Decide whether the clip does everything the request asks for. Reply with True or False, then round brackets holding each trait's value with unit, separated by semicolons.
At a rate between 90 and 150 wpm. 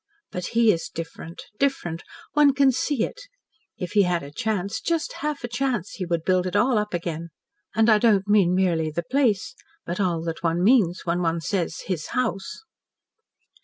False (185 wpm)